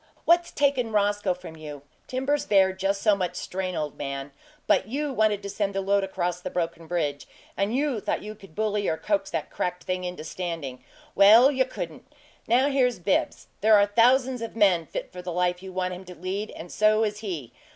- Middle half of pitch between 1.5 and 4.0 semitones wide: Yes, average, 3.7 semitones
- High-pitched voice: Yes, high, 195 Hz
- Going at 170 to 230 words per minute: Yes, fast, 205 wpm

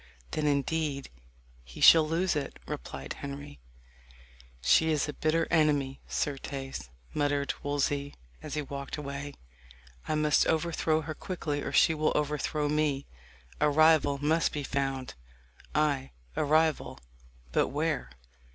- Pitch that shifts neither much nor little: No, narrow, 1.9 semitones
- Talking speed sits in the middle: No, slow, 130 wpm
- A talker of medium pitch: Yes, medium, 145 Hz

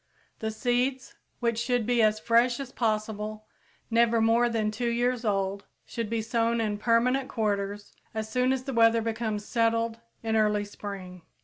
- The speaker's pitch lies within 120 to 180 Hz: No, high, 230 Hz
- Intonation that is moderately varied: No, narrow, 1.8 semitones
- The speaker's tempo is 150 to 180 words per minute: Yes, average, 170 wpm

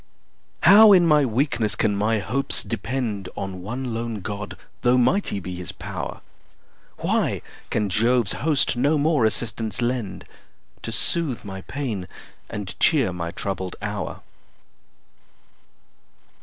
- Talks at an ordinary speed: No, slow, 125 wpm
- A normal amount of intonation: Yes, average, 4.8 semitones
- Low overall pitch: Yes, low, 115 Hz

